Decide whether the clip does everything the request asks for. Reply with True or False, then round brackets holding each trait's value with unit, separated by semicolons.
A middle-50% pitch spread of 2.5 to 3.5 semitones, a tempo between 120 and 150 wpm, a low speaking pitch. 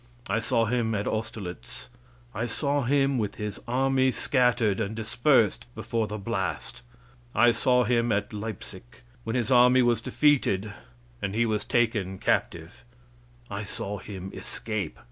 True (3.2 semitones; 145 wpm; 115 Hz)